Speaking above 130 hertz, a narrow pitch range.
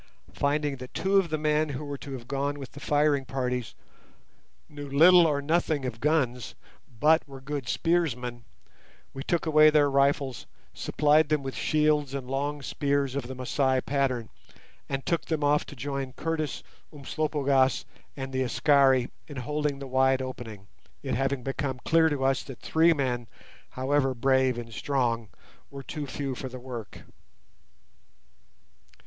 Yes: medium, 140 Hz; narrow, 2.3 semitones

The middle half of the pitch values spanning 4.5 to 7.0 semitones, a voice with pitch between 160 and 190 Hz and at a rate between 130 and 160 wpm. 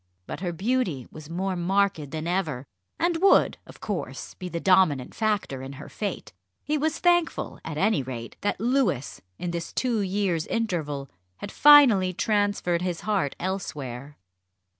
Yes: wide, 5.6 semitones; medium, 185 Hz; average, 155 wpm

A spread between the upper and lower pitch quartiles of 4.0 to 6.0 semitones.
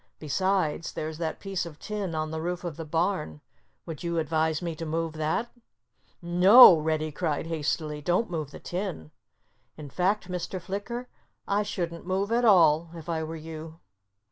No: average, 3.1 semitones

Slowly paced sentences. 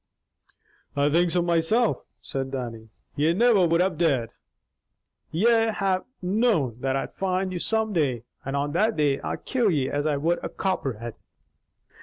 No: average, 160 wpm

